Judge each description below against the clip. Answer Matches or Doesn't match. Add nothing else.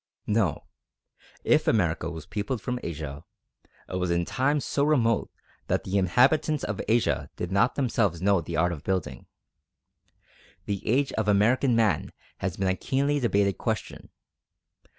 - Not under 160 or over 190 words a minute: Doesn't match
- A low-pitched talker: Matches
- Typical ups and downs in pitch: Doesn't match